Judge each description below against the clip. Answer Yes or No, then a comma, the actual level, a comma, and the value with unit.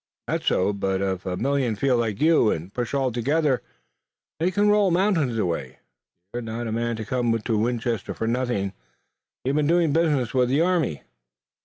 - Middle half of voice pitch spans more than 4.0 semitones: Yes, wide, 5.4 semitones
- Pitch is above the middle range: No, low, 120 Hz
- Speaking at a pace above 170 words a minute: Yes, average, 180 wpm